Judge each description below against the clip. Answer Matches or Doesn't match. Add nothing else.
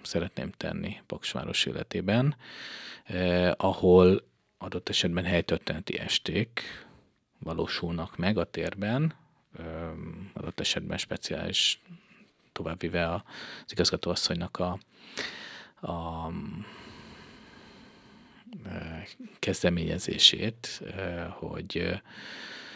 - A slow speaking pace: Matches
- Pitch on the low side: Matches